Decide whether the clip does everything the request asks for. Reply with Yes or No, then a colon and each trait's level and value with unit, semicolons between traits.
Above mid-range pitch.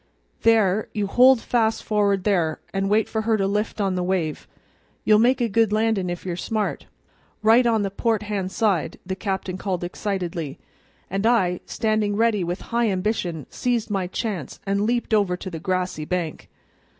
Yes: high, 200 Hz